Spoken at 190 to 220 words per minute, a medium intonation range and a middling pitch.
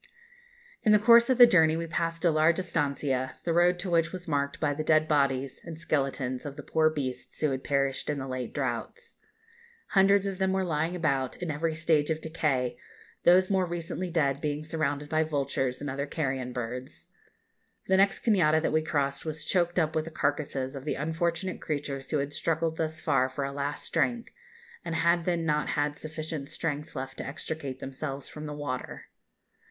Yes: average, 195 wpm; average, 3.2 semitones; medium, 155 Hz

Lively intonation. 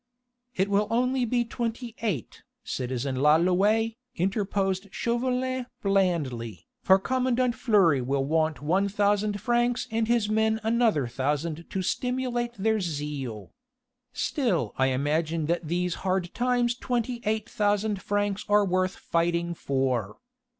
Yes: wide, 6.6 semitones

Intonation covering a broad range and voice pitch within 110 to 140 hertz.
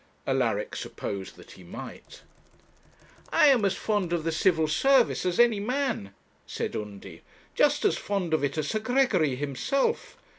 No: wide, 8.1 semitones; medium, 180 Hz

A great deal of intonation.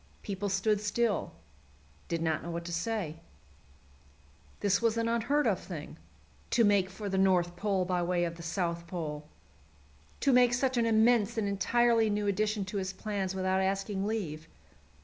No: average, 3.9 semitones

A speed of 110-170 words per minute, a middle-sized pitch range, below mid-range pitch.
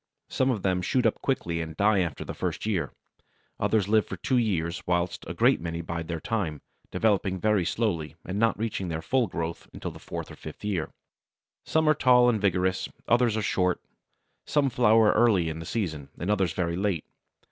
No: average, 195 wpm; average, 4.8 semitones; very low, 95 Hz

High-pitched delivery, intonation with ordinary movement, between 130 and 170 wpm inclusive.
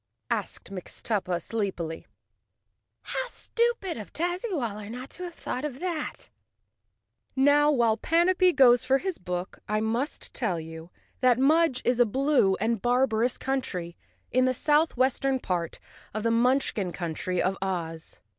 No: high, 245 Hz; wide, 7.1 semitones; slow, 135 wpm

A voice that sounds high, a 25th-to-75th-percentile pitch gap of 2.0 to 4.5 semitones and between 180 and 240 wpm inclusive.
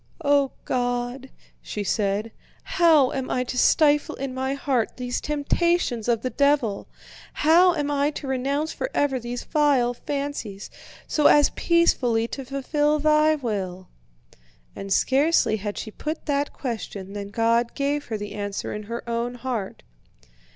No: very high, 260 Hz; average, 4.2 semitones; average, 145 wpm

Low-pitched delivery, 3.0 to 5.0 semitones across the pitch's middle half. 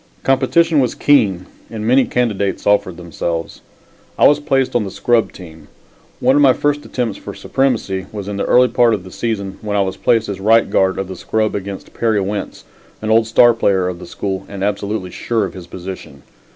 Yes: low, 105 Hz; average, 4.1 semitones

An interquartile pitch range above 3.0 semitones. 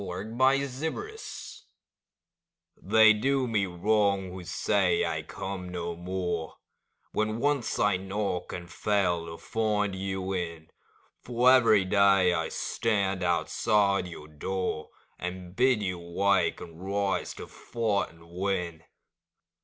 Yes: average, 3.4 semitones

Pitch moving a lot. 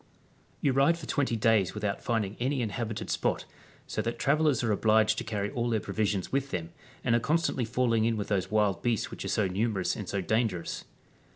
No: average, 3.0 semitones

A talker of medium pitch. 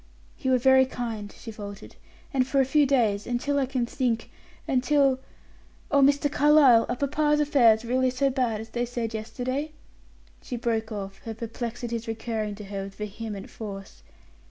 No: high, 240 Hz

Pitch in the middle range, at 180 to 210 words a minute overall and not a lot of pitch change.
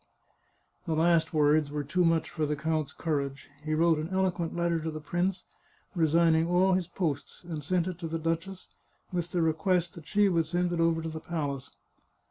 Yes: medium, 165 Hz; average, 195 wpm; narrow, 2.0 semitones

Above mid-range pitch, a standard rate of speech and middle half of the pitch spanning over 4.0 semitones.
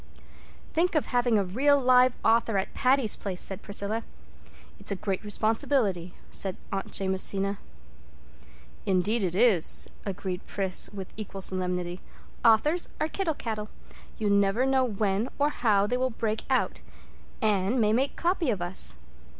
Yes: high, 215 Hz; average, 150 wpm; average, 4.5 semitones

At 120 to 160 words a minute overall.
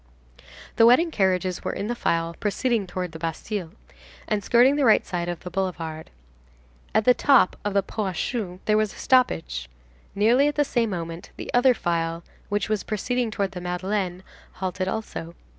No: average, 180 wpm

